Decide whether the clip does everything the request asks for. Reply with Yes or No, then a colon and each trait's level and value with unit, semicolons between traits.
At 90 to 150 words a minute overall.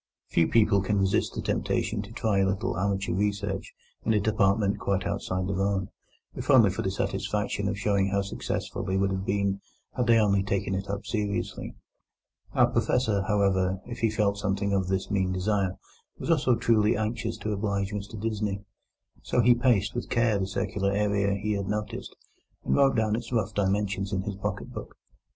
No: average, 185 wpm